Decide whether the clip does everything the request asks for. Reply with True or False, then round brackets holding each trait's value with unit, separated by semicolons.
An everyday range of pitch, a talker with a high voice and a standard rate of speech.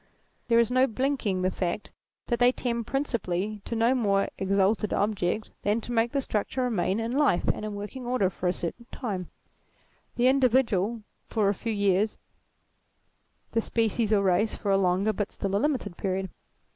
True (3.5 semitones; 215 Hz; 175 wpm)